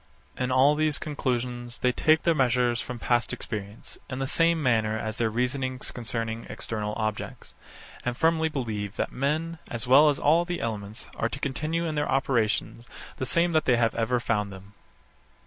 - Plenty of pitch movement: No, average, 4.6 semitones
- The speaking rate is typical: Yes, average, 180 wpm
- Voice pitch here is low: Yes, low, 125 Hz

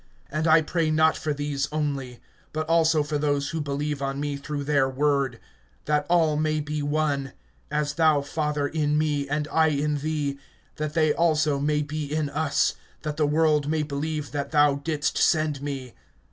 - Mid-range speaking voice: Yes, medium, 150 Hz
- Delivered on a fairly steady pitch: Yes, narrow, 1.5 semitones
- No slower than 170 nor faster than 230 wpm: Yes, average, 180 wpm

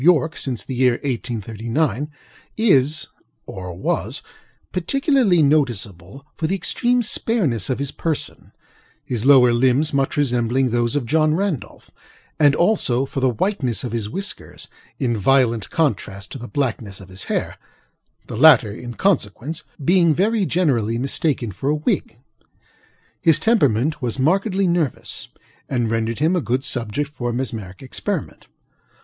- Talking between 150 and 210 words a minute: No, slow, 135 wpm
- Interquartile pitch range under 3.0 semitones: No, average, 5.3 semitones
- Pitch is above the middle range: No, low, 135 Hz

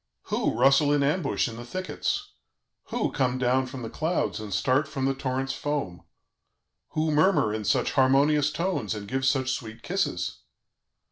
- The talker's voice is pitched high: No, low, 135 Hz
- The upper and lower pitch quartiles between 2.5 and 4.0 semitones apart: Yes, average, 3.7 semitones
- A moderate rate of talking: Yes, average, 160 wpm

